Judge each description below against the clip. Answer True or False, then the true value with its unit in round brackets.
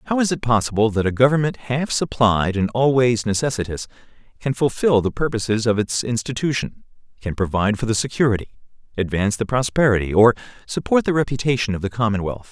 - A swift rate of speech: False (165 wpm)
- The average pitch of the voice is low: True (115 Hz)